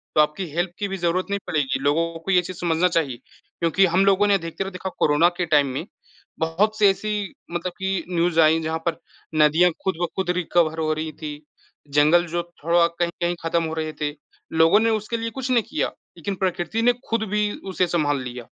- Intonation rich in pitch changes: No, average, 3.3 semitones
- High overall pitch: No, medium, 175 Hz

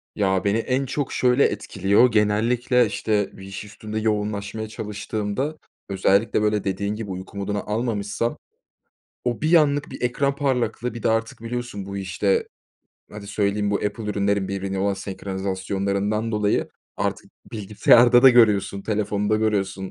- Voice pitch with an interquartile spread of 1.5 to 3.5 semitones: Yes, narrow, 2.5 semitones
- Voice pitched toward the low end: Yes, low, 105 Hz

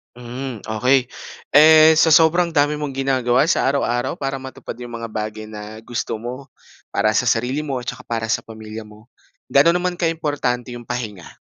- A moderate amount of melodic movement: Yes, average, 4.3 semitones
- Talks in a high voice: No, low, 125 Hz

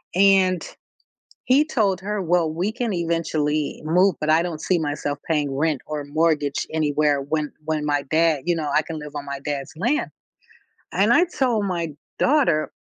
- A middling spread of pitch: Yes, average, 3.9 semitones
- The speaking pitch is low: No, medium, 160 Hz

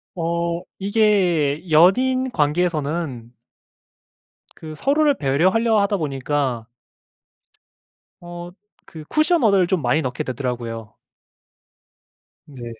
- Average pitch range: No, wide, 6.1 semitones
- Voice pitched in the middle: Yes, medium, 170 Hz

